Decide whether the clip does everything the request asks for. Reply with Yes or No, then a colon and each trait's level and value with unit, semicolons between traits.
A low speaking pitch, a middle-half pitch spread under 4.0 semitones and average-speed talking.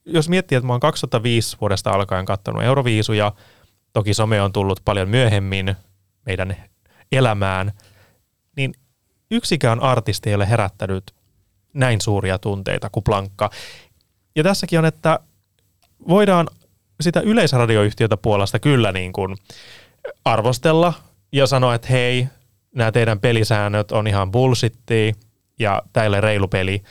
No: low, 110 Hz; average, 4.3 semitones; average, 125 wpm